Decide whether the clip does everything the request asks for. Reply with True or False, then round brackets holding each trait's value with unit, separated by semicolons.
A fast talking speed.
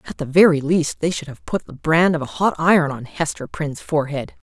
True (240 wpm)